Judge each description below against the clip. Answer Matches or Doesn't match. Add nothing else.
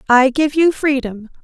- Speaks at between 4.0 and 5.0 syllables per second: Matches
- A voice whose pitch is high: Matches